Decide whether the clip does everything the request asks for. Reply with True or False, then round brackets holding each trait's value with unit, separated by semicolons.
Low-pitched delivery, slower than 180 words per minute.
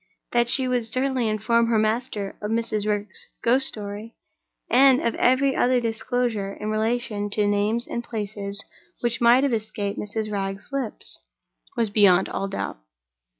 False (220 Hz; 150 wpm)